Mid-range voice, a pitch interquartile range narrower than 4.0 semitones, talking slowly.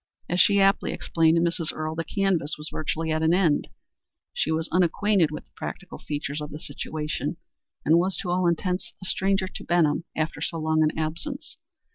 No: medium, 165 Hz; average, 2.7 semitones; average, 190 wpm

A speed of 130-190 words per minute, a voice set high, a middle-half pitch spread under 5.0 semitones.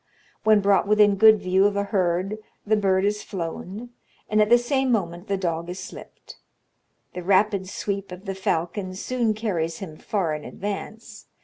Yes: average, 175 wpm; high, 200 Hz; narrow, 2.6 semitones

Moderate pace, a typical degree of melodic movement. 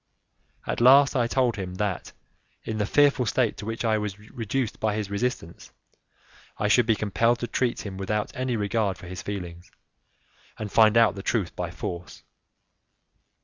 Yes: average, 170 wpm; average, 3.4 semitones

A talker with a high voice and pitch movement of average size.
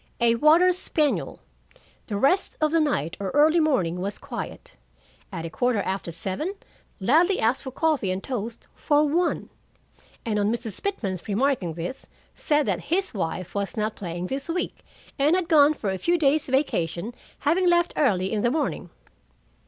No: very high, 260 Hz; wide, 7.8 semitones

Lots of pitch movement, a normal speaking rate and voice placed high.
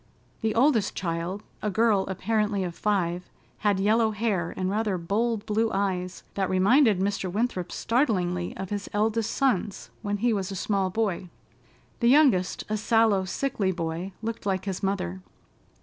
No: average, 3.0 semitones; average, 155 wpm; high, 200 Hz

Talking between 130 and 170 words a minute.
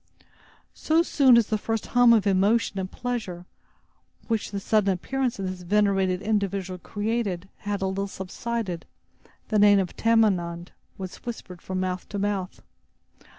Yes: average, 150 wpm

